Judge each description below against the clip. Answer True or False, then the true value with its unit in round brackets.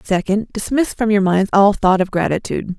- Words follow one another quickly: False (195 wpm)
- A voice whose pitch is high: True (200 Hz)